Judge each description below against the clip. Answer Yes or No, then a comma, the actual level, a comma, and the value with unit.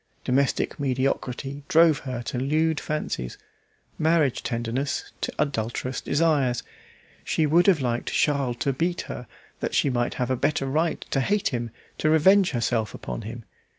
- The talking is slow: No, average, 150 wpm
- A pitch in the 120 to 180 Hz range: Yes, low, 135 Hz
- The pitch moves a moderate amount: Yes, average, 4.2 semitones